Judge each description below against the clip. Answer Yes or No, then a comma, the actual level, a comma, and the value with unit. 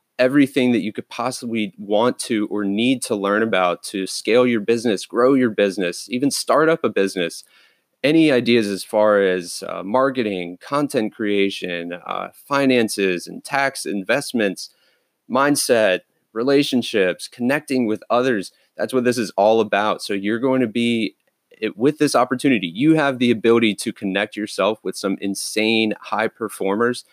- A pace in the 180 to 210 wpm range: No, average, 155 wpm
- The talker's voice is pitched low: Yes, low, 115 Hz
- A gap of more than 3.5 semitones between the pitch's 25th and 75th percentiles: Yes, average, 4.3 semitones